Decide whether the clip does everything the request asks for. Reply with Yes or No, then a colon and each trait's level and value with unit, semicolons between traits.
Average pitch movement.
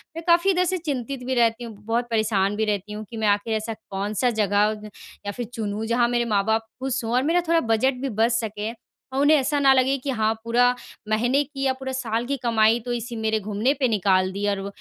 Yes: average, 3.5 semitones